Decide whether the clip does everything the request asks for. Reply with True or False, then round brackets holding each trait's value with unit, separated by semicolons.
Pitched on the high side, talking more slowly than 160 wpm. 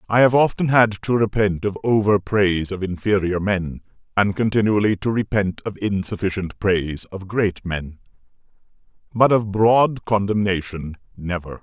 False (100 Hz; 140 wpm)